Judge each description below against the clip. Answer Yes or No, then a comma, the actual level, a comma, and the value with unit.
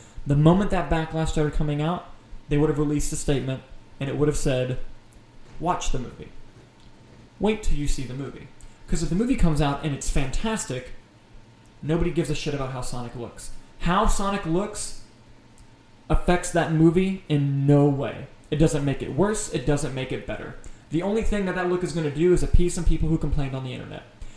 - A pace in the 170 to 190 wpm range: No, average, 200 wpm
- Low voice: No, medium, 150 Hz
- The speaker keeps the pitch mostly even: No, average, 5.0 semitones